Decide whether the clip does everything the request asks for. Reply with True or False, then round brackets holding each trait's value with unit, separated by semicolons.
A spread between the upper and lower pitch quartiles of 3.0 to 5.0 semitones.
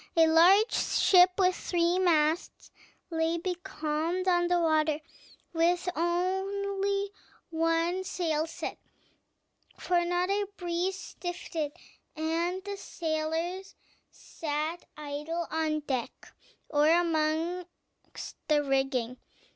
False (2.5 semitones)